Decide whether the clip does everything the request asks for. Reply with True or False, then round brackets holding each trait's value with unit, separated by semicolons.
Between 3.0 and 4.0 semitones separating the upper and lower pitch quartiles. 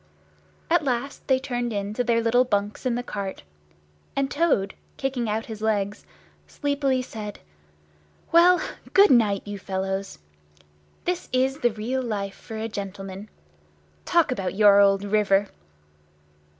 False (4.6 semitones)